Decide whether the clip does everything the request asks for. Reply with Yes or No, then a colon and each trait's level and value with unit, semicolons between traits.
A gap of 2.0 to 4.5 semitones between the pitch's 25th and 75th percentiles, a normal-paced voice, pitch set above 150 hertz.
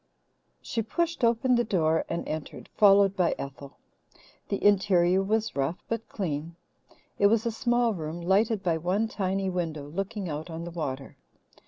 No: average, 4.9 semitones; average, 160 wpm; high, 190 Hz